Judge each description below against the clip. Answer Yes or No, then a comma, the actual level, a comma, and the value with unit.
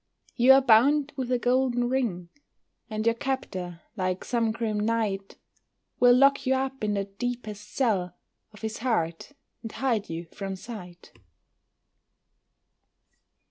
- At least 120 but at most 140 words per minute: Yes, slow, 135 wpm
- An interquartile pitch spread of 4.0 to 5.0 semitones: Yes, average, 4.4 semitones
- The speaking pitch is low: No, high, 230 Hz